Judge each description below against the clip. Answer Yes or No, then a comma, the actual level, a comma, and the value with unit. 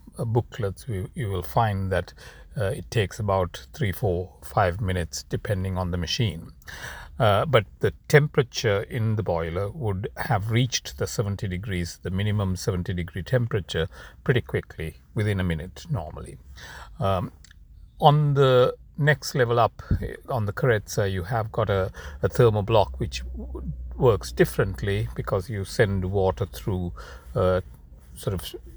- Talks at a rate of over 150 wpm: No, average, 140 wpm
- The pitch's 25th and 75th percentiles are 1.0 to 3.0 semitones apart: No, average, 4.3 semitones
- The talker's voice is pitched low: Yes, very low, 95 Hz